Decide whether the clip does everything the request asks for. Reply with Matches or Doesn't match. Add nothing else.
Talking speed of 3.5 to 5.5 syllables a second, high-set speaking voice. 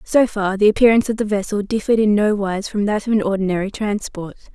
Doesn't match